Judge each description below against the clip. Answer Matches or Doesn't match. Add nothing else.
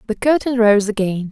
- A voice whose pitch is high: Matches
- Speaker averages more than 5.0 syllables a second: Matches